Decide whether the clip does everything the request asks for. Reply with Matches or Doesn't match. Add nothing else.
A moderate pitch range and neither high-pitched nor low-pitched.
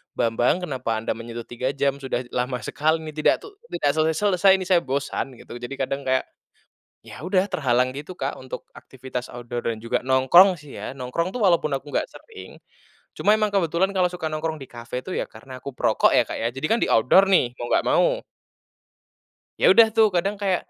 Doesn't match